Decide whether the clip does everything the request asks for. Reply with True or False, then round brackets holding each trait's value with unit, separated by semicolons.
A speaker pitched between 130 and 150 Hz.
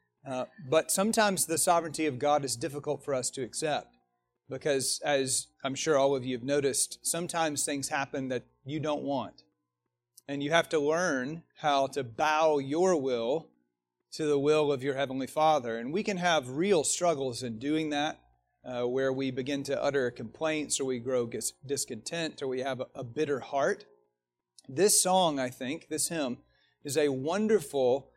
True (140 Hz)